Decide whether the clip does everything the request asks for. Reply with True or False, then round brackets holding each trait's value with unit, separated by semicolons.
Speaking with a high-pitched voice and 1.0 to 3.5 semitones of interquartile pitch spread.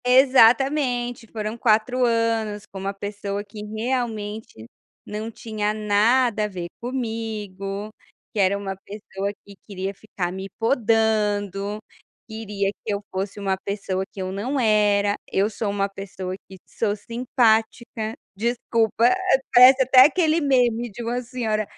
True (215 Hz; 2.8 semitones)